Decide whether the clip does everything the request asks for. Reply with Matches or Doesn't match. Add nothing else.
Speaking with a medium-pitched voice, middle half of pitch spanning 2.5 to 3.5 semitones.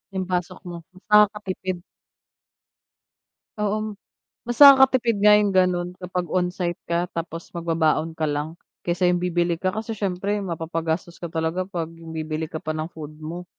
Matches